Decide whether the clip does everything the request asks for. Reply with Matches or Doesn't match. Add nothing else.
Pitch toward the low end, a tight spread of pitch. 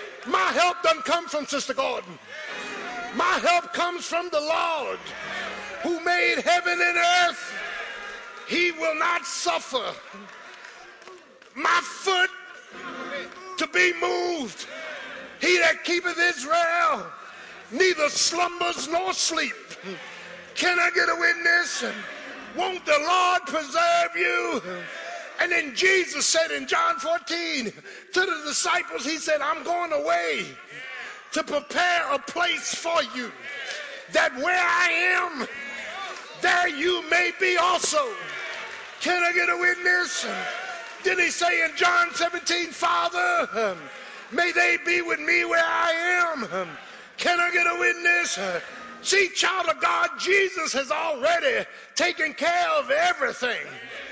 Doesn't match